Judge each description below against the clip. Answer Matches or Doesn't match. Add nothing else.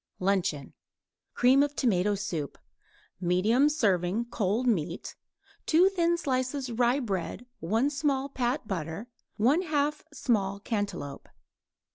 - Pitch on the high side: Matches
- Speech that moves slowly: Matches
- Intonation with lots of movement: Matches